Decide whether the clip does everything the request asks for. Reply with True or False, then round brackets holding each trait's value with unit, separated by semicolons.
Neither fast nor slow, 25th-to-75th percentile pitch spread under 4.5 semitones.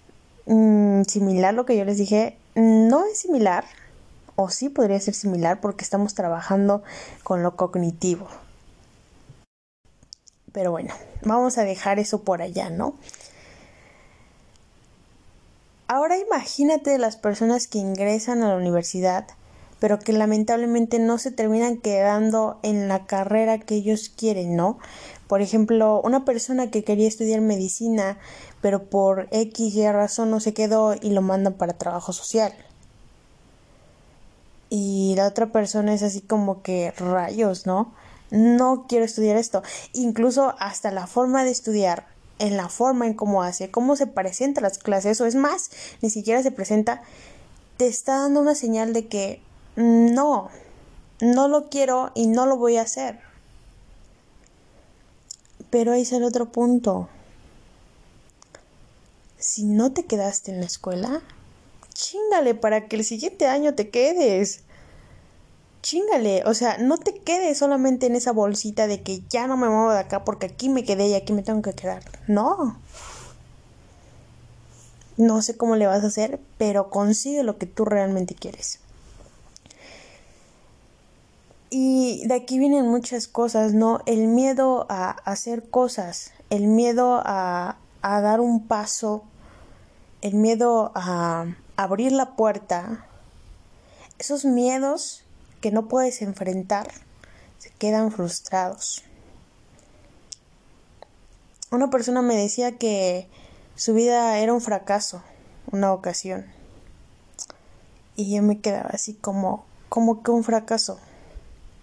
True (135 wpm; 3.4 semitones)